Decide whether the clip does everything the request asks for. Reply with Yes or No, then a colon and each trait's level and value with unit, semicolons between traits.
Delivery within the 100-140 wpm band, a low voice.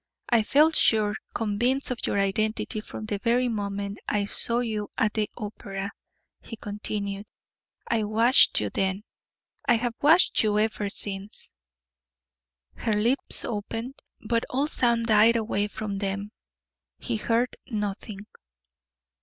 No: slow, 135 wpm; high, 215 Hz